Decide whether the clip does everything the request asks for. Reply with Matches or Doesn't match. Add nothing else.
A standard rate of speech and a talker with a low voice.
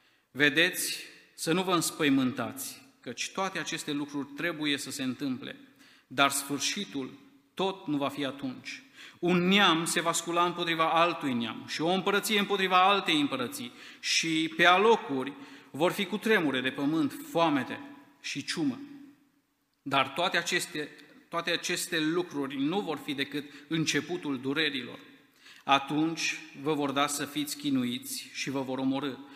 Doesn't match